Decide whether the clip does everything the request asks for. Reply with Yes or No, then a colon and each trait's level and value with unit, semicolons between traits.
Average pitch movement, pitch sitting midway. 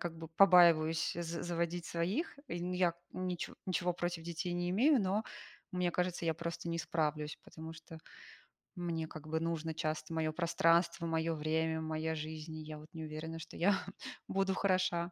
No: narrow, 1.7 semitones; medium, 165 Hz